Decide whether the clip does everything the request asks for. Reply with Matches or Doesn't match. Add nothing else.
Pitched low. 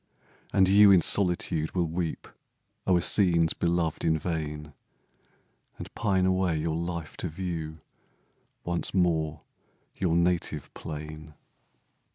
Matches